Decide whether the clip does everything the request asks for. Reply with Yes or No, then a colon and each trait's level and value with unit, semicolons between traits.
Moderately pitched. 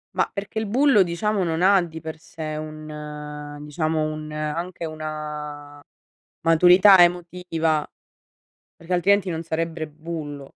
Yes: medium, 160 Hz